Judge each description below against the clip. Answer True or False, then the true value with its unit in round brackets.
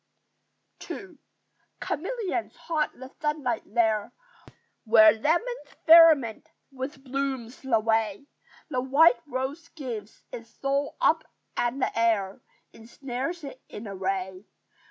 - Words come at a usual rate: False (115 wpm)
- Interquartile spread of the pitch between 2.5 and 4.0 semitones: False (5.2 semitones)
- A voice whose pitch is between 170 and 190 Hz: False (260 Hz)